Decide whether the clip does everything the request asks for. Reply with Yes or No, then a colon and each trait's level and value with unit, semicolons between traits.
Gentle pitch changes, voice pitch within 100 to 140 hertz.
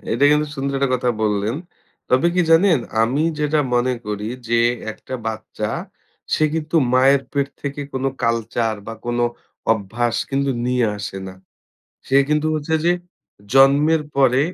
No: average, 3.9 semitones; low, 135 Hz